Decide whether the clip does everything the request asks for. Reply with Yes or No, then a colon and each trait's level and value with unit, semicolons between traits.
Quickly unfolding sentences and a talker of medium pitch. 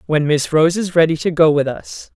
Yes: fast, 245 wpm; medium, 160 Hz